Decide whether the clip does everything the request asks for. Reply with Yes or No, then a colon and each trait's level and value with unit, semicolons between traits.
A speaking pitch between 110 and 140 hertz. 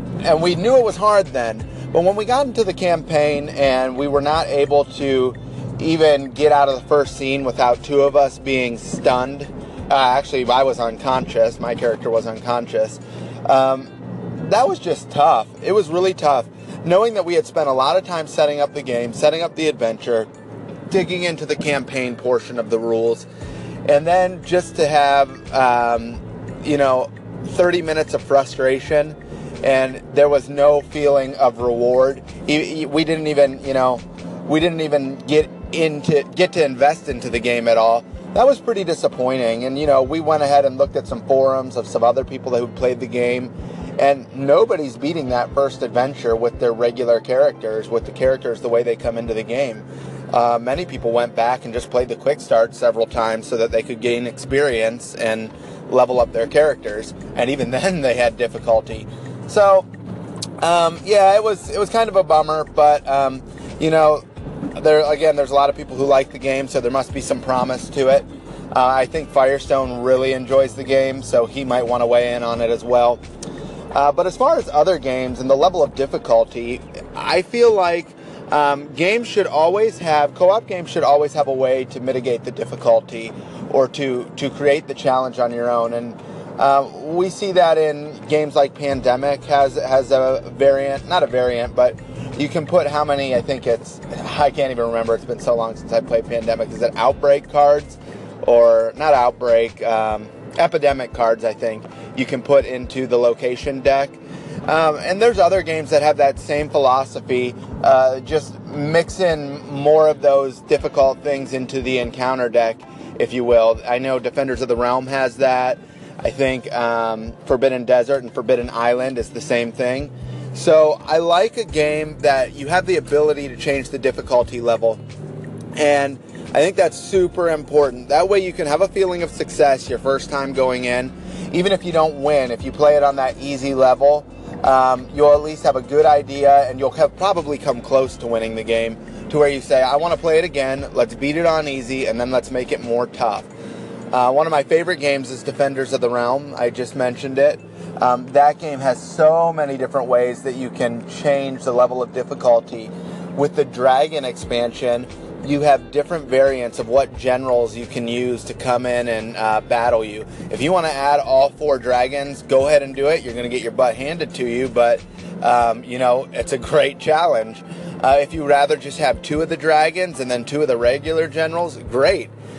Yes: low, 135 Hz